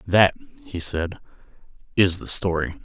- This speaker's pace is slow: Yes, slow, 125 wpm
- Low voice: Yes, very low, 85 Hz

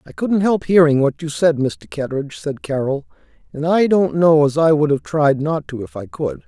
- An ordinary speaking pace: No, fast, 230 wpm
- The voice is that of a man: Yes, male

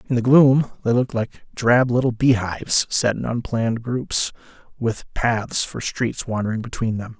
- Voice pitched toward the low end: Yes, low, 120 Hz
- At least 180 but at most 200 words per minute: No, average, 165 wpm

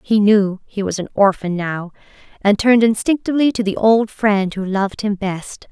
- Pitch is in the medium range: No, high, 205 Hz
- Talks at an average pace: Yes, average, 190 wpm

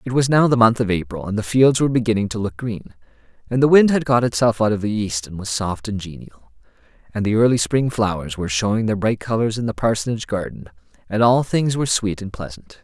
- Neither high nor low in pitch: No, low, 110 Hz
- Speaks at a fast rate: Yes, fast, 240 wpm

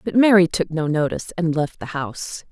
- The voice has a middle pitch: Yes, medium, 170 Hz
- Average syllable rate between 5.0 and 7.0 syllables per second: Yes, 5.5 syllables/s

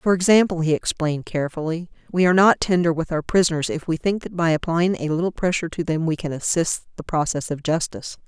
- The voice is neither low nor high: Yes, medium, 165 Hz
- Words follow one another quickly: Yes, fast, 215 wpm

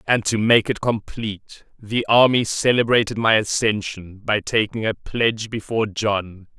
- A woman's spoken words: No, male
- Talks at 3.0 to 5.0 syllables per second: Yes, 4.7 syllables/s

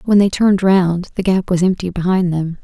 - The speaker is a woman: Yes, female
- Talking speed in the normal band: No, fast, 230 wpm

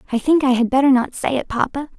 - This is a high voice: Yes, very high, 260 Hz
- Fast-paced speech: Yes, fast, 270 wpm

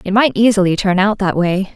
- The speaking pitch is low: No, high, 195 Hz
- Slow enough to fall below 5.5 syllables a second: No, 5.6 syllables/s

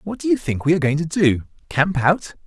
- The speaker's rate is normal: No, fast, 245 wpm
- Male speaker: Yes, male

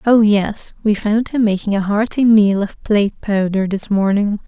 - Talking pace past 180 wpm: No, average, 175 wpm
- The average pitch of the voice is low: No, high, 210 Hz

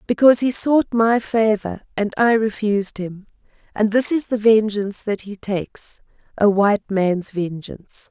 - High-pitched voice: Yes, high, 210 Hz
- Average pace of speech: Yes, average, 150 wpm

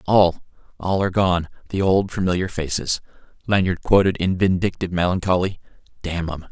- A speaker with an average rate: No, slow, 130 wpm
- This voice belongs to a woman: No, male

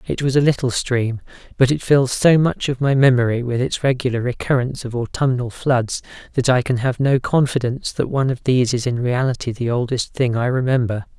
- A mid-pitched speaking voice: No, low, 125 Hz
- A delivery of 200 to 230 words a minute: Yes, fast, 205 wpm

